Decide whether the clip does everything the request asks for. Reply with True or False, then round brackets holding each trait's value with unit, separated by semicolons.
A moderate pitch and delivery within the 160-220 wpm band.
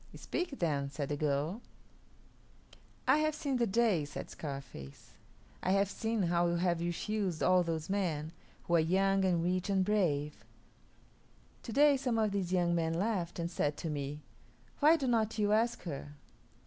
True (180 Hz; 170 wpm)